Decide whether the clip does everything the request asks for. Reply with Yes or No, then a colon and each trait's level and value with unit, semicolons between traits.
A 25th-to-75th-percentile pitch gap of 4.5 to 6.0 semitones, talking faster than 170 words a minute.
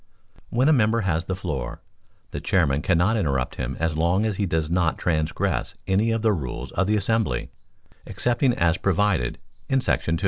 Yes: average, 5.1 semitones; average, 180 wpm